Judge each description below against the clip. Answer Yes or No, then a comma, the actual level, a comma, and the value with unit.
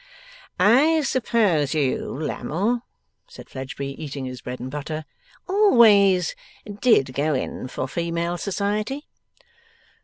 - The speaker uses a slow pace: Yes, slow, 110 wpm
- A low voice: No, medium, 170 Hz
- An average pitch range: No, wide, 8.4 semitones